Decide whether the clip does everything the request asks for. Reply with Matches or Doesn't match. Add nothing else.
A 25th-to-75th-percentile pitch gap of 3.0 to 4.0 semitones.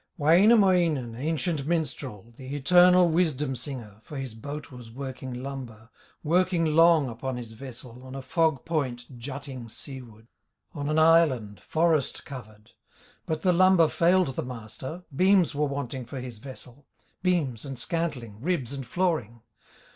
Doesn't match